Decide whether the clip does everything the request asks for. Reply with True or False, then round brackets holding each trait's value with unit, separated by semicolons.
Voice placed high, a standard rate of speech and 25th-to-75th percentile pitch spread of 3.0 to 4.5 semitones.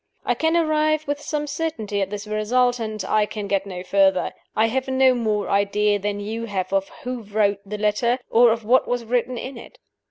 False (220 Hz; 210 wpm; 3.7 semitones)